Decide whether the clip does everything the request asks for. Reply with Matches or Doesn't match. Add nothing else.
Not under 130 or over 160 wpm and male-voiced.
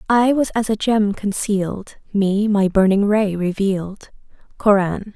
Doesn't match